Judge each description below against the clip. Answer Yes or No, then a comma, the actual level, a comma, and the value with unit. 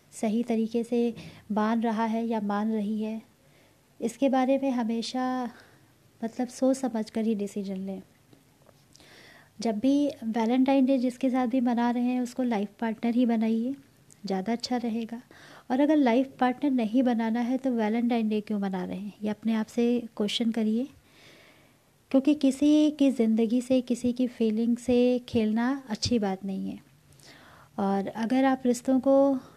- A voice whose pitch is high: Yes, high, 235 Hz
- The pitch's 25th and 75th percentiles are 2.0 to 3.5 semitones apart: Yes, narrow, 2.6 semitones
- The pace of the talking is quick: No, average, 160 wpm